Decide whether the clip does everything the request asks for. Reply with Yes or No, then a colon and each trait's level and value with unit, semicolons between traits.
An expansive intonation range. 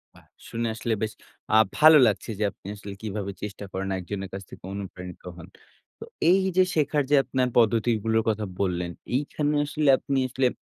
Yes: wide, 5.7 semitones